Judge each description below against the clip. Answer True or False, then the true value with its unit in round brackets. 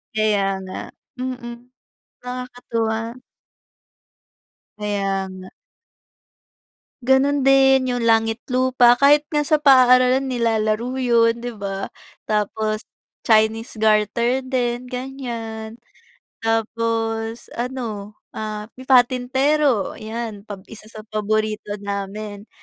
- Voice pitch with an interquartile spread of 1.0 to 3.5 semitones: True (2.8 semitones)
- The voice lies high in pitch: True (230 Hz)